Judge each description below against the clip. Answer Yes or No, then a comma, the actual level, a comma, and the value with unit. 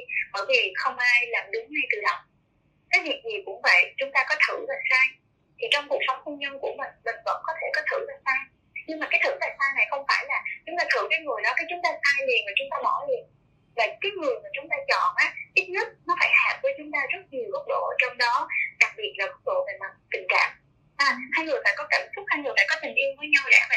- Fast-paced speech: Yes, fast, 275 wpm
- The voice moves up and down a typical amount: No, wide, 6.7 semitones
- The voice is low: No, very high, 300 Hz